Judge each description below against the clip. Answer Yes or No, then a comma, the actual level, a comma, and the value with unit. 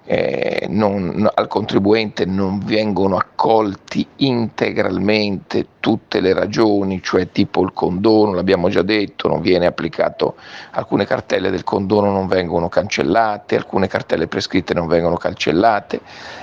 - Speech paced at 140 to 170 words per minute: No, average, 120 wpm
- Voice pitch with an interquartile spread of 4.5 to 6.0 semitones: No, narrow, 2.6 semitones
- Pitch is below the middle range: Yes, low, 100 Hz